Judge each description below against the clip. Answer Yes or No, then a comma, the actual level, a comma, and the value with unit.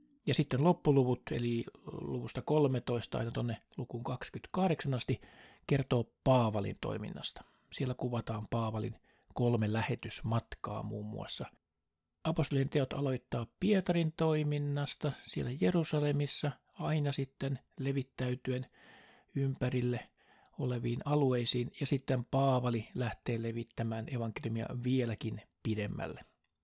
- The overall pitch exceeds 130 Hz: No, low, 125 Hz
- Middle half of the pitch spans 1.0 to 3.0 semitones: No, average, 3.7 semitones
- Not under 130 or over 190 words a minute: No, slow, 95 wpm